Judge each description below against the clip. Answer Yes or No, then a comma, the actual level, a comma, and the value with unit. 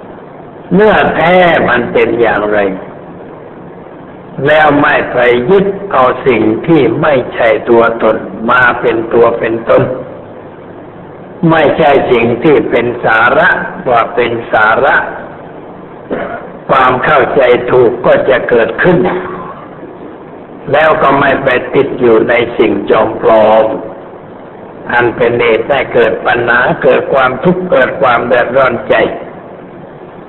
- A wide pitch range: Yes, wide, 6.0 semitones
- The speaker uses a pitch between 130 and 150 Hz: No, low, 115 Hz